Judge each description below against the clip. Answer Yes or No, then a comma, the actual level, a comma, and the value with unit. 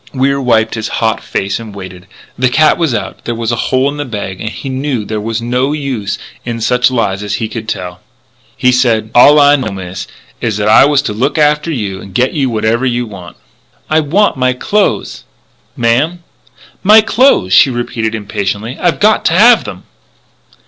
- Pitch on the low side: Yes, low, 120 Hz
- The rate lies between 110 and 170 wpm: No, average, 195 wpm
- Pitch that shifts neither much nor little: Yes, average, 4.8 semitones